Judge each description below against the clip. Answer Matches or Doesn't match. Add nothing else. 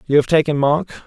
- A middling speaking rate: Doesn't match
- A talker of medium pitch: Matches